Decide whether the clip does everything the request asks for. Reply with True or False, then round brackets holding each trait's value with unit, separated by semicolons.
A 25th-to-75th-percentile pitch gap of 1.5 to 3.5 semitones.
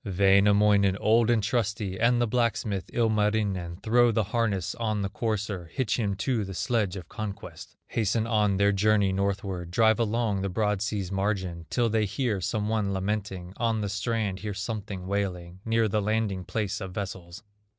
True (2.4 semitones)